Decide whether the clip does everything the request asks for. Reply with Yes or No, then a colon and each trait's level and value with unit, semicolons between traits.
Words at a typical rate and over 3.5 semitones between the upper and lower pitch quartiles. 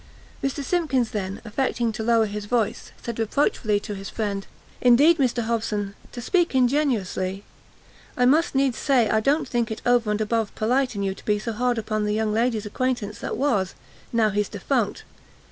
No: average, 180 wpm; average, 3.2 semitones